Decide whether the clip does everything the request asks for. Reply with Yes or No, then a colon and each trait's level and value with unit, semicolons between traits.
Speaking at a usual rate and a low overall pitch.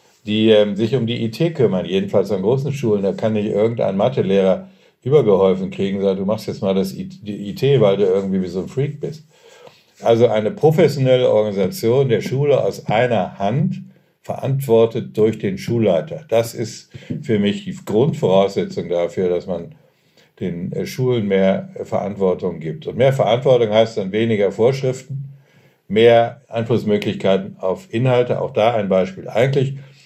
Yes: average, 160 wpm; low, 115 Hz